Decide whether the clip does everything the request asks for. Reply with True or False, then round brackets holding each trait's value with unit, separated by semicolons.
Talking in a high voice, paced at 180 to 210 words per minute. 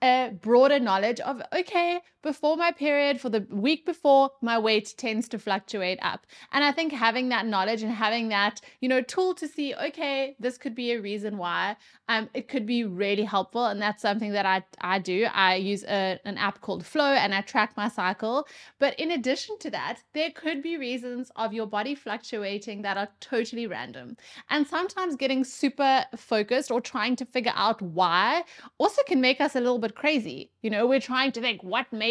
True (240 Hz; 200 wpm)